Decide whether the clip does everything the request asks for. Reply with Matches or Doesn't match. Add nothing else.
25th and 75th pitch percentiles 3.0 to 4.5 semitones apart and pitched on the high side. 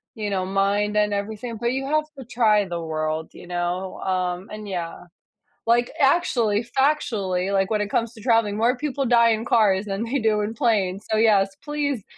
Matches